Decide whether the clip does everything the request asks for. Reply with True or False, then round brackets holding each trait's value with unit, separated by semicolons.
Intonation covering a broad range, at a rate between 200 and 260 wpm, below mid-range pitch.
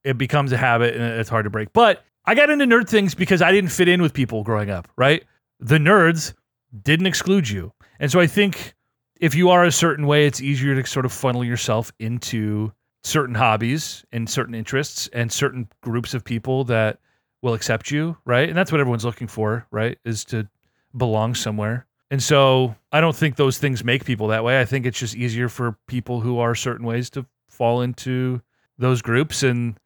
False (3.8 semitones; 205 wpm; 125 Hz)